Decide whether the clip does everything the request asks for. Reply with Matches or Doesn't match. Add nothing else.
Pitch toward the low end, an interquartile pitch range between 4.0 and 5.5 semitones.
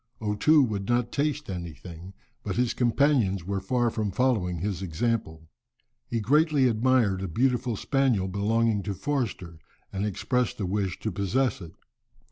Matches